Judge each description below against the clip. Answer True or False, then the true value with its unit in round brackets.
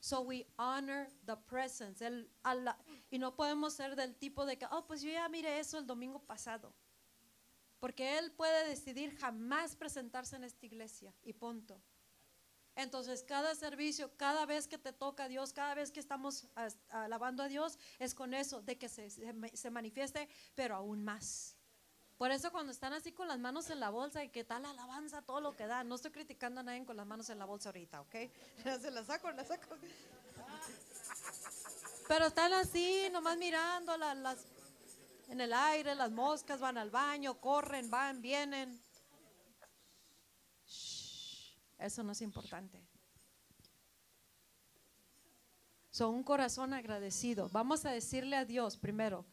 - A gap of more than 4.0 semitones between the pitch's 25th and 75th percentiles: False (3.7 semitones)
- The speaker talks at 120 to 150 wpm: False (160 wpm)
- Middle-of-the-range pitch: False (265 Hz)